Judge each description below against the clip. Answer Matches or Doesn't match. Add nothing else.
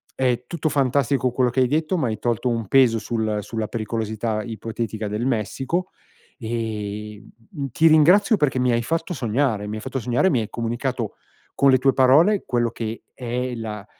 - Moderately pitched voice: Doesn't match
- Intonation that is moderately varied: Matches